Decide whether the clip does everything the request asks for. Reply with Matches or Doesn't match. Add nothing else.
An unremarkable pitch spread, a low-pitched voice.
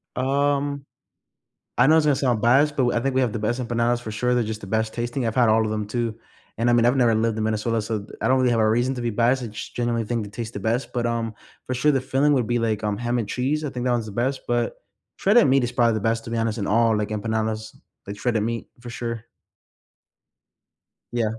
Doesn't match